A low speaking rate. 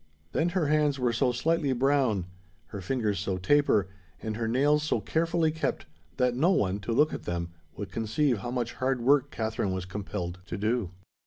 No: average, 185 wpm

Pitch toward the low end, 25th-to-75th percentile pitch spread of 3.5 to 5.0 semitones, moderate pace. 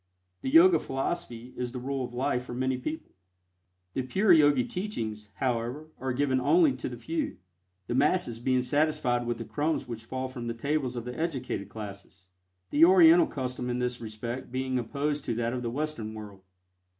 Yes: low, 130 Hz; average, 4.0 semitones; average, 185 wpm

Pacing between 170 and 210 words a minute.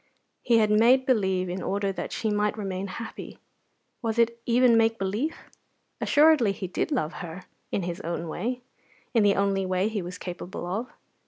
Yes: average, 175 wpm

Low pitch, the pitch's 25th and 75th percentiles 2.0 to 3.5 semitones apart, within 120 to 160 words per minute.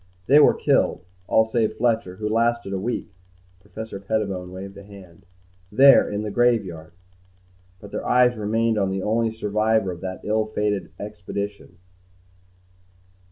Yes: low, 105 Hz; narrow, 2.4 semitones; average, 150 wpm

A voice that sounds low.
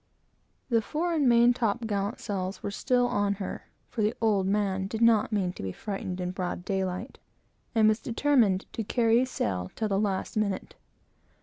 No: high, 210 Hz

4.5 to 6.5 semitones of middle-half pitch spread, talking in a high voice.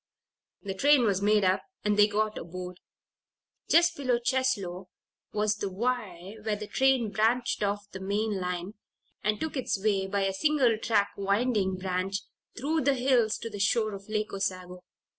No: average, 3.6 semitones; high, 210 Hz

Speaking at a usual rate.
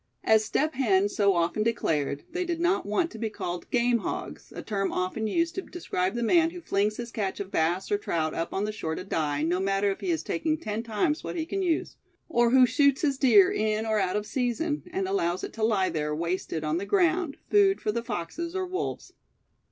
No: fast, 230 wpm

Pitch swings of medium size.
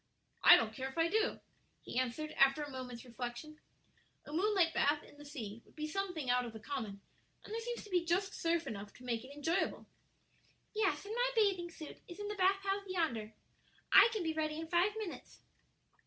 No: wide, 7.1 semitones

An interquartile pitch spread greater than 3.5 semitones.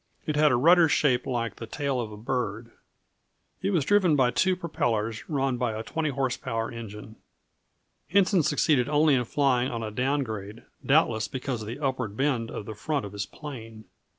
Yes: average, 4.7 semitones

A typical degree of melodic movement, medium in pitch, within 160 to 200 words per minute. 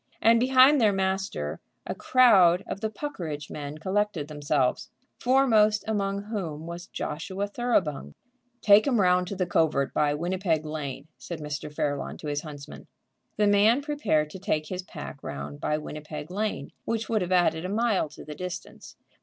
No: wide, 5.7 semitones; medium, 180 Hz; average, 165 wpm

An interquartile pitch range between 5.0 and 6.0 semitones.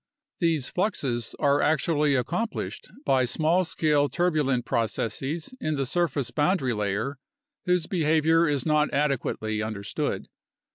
No: average, 4.2 semitones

